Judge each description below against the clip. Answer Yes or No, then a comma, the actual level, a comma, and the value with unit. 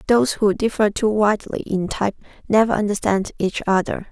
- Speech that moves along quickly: No, average, 160 wpm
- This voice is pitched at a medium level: No, high, 205 Hz